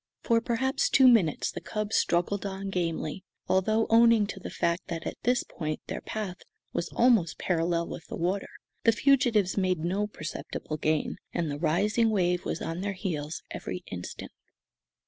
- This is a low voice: No, high, 190 Hz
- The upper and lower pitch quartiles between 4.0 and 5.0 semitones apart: Yes, average, 4.4 semitones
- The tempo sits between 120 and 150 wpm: No, average, 165 wpm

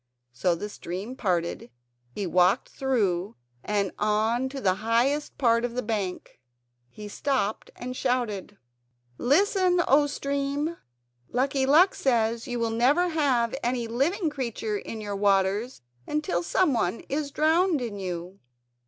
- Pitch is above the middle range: Yes, high, 235 Hz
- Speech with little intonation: No, wide, 5.4 semitones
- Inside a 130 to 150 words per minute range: Yes, slow, 135 wpm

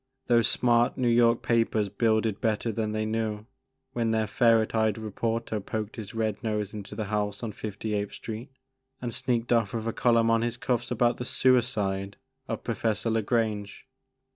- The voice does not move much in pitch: Yes, narrow, 1.7 semitones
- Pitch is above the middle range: No, low, 110 Hz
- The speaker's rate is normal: Yes, average, 180 wpm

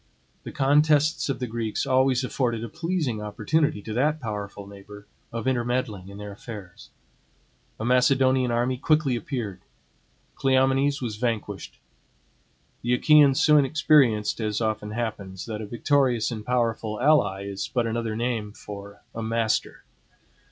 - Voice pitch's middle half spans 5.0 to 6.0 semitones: No, average, 3.8 semitones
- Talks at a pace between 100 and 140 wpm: Yes, slow, 135 wpm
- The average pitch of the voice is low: Yes, low, 120 Hz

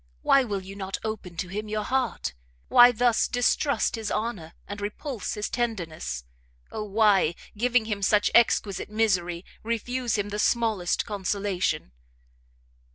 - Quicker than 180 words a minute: No, average, 140 wpm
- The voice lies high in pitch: Yes, high, 210 Hz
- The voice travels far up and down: No, average, 3.2 semitones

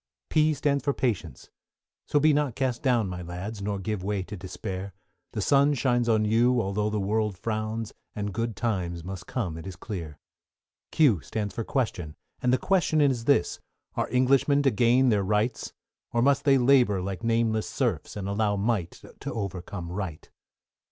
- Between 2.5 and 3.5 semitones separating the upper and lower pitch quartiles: No, average, 4.5 semitones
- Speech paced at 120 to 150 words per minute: No, average, 175 wpm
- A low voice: Yes, low, 110 Hz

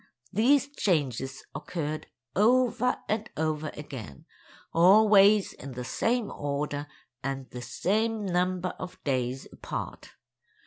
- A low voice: No, medium, 175 Hz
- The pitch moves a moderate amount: No, wide, 7.6 semitones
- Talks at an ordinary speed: No, slow, 100 wpm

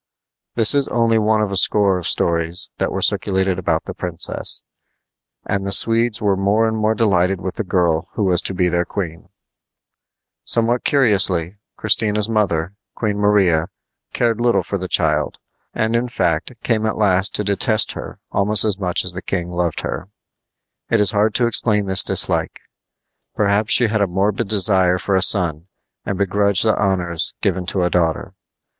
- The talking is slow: No, average, 175 wpm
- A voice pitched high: No, low, 100 Hz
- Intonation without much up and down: No, average, 3.2 semitones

